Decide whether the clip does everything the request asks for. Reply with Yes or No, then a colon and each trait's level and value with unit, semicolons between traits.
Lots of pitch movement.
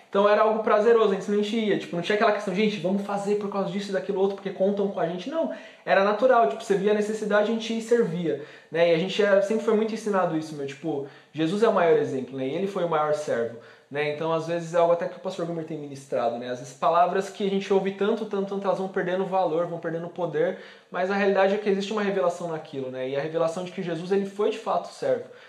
No: average, 3.7 semitones